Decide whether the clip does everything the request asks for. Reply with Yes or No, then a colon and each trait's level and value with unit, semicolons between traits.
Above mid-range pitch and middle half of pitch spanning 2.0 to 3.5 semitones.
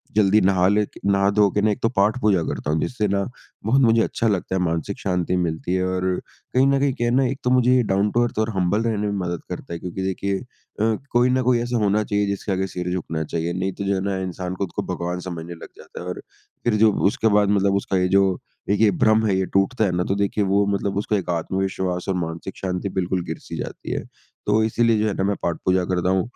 No: low, 100 Hz; average, 2.9 semitones